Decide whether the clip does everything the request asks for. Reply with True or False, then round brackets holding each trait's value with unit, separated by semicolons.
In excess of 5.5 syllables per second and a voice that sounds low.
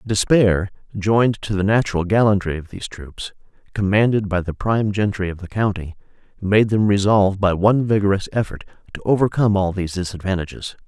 True (6.0 syllables/s; 100 Hz)